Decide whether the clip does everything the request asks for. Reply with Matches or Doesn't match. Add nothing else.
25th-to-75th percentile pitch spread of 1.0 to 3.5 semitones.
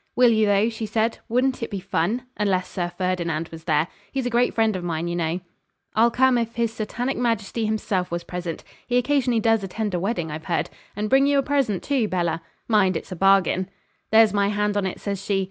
Doesn't match